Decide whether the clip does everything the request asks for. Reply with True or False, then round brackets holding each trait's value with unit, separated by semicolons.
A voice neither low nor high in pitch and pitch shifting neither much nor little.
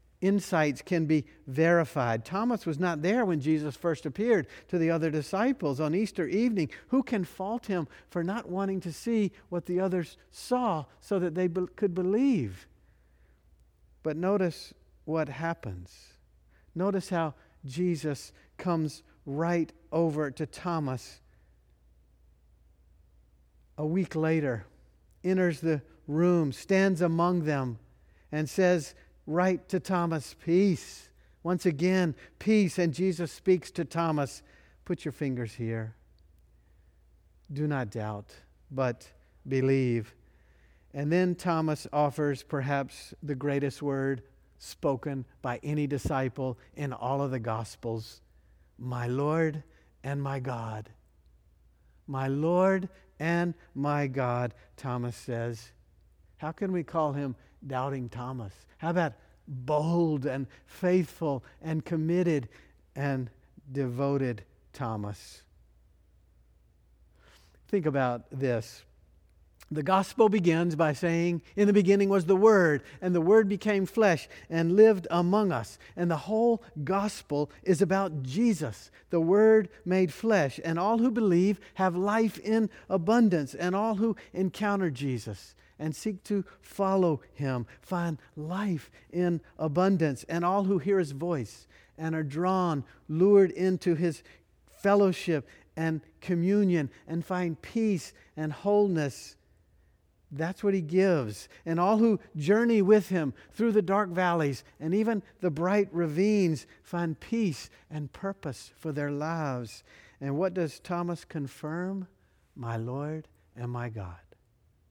False (155 Hz; 7.1 semitones)